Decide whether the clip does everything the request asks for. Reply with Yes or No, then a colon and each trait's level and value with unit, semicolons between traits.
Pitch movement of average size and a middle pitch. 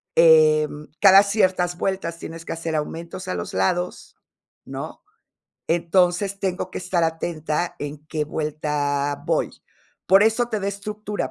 Yes: average, 3.9 semitones; medium, 170 Hz